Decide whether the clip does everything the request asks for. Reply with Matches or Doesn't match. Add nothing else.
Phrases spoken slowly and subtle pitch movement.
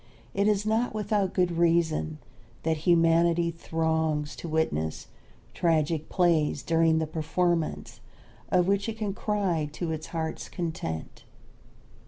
Matches